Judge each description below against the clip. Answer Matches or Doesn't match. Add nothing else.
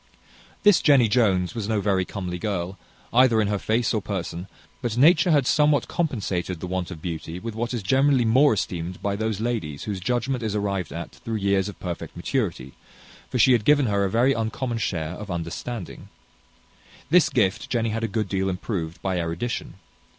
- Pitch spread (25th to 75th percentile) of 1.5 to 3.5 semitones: Doesn't match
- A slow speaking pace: Doesn't match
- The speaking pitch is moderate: Doesn't match